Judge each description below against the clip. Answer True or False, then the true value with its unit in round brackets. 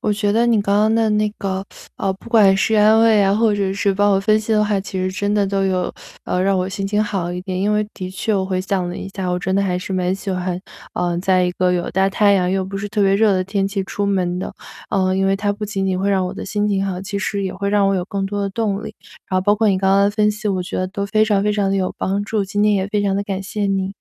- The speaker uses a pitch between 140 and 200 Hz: True (195 Hz)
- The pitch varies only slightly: True (1.6 semitones)